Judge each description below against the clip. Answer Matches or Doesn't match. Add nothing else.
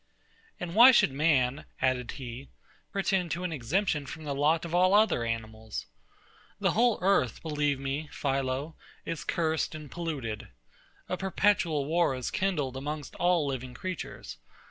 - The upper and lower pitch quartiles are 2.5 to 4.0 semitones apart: Doesn't match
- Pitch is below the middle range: Doesn't match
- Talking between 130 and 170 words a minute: Matches